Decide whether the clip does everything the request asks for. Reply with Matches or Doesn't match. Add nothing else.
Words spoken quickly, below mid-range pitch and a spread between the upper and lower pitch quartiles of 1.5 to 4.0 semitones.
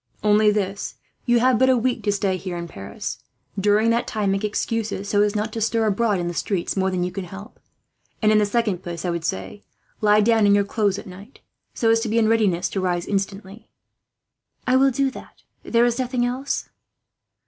Doesn't match